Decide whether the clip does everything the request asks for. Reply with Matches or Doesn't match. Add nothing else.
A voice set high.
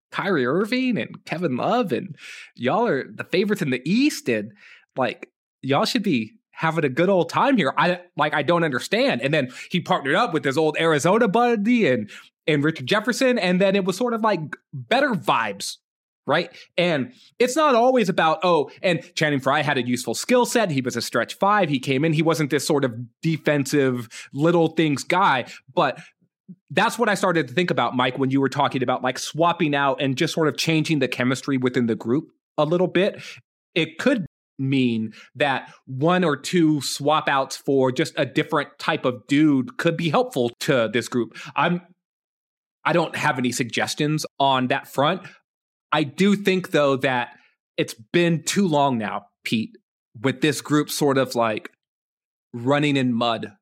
Doesn't match